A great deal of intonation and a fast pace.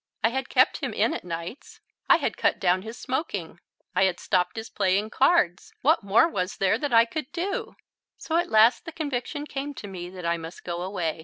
Yes: wide, 7.3 semitones; fast, 215 wpm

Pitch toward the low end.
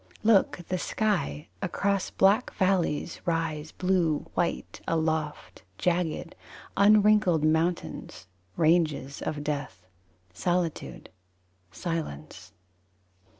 No: medium, 165 Hz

